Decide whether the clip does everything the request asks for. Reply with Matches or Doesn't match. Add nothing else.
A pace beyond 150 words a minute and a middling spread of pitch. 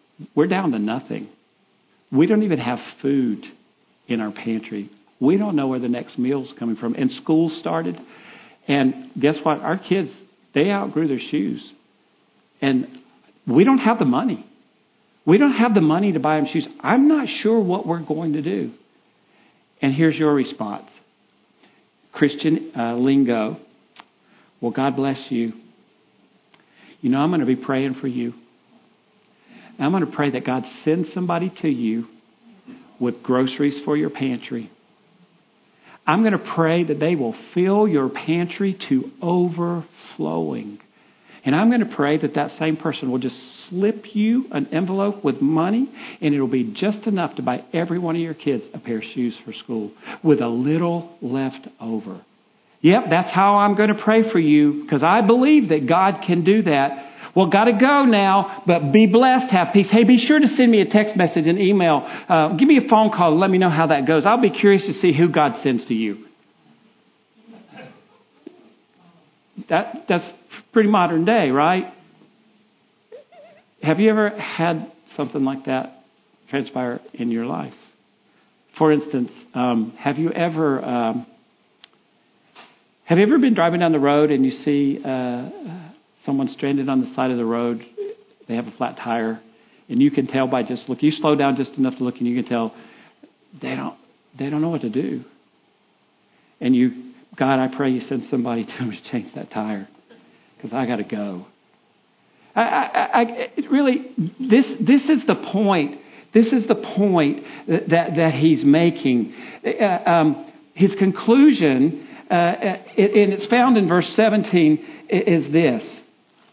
Doesn't match